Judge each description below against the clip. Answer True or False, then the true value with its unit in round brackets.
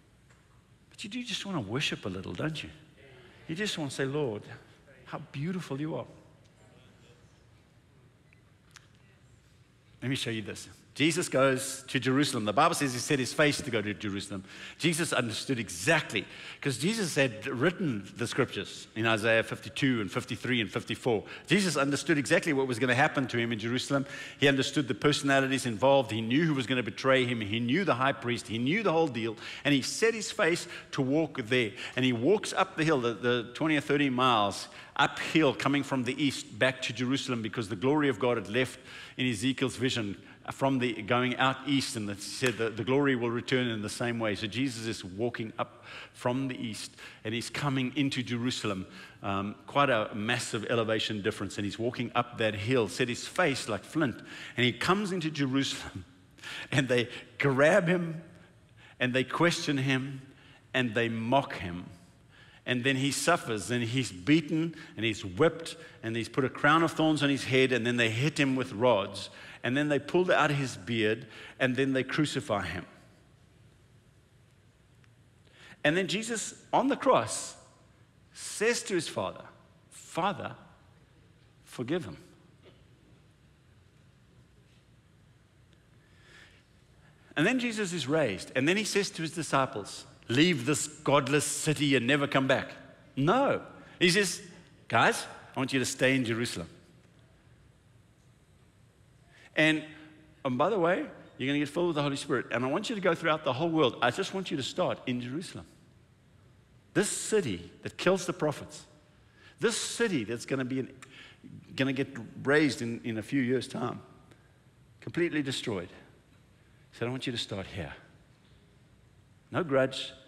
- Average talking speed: True (170 wpm)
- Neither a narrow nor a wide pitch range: True (3.9 semitones)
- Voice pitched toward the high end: False (130 Hz)